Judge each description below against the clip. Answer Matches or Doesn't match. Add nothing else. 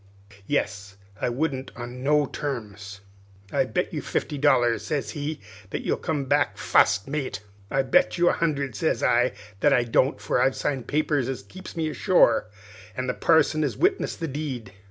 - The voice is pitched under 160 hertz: Matches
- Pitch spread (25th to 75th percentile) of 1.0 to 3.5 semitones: Doesn't match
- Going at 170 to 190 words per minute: Matches